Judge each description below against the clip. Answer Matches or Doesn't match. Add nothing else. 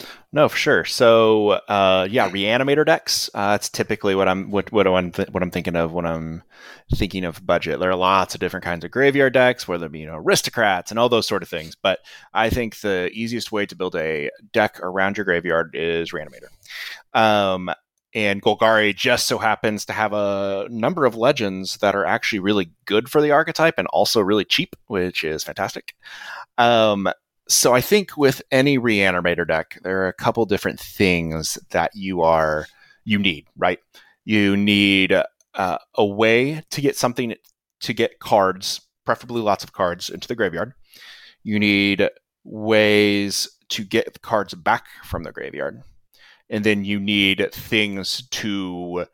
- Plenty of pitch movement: Doesn't match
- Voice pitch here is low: Matches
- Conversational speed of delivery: Matches